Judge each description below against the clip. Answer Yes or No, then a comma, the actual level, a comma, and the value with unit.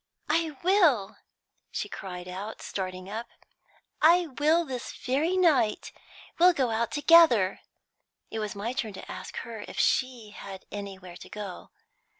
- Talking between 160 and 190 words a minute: No, average, 150 wpm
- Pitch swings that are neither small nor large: No, wide, 7.7 semitones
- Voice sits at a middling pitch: No, high, 230 Hz